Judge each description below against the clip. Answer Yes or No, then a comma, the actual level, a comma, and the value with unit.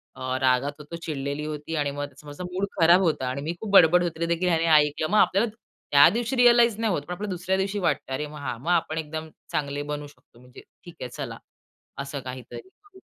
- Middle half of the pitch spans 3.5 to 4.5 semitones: Yes, average, 4.1 semitones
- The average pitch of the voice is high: No, medium, 155 Hz